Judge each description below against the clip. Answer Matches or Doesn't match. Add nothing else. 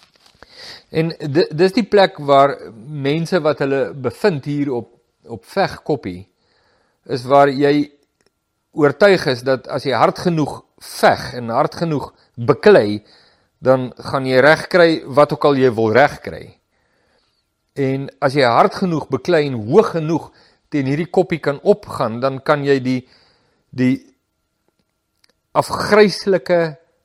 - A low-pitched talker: Doesn't match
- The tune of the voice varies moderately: Matches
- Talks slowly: Matches